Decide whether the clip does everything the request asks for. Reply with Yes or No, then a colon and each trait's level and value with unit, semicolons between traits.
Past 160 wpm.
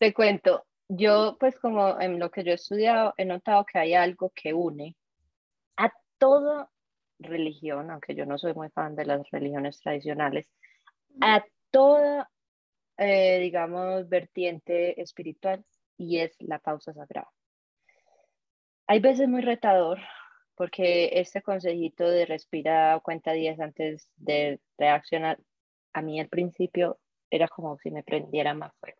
No: average, 140 wpm